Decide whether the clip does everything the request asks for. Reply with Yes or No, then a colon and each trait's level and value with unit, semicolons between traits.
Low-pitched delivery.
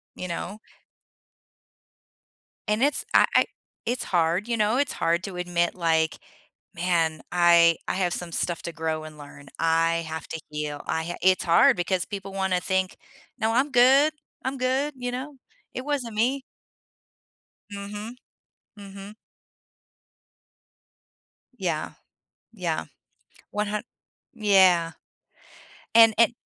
No: high, 190 Hz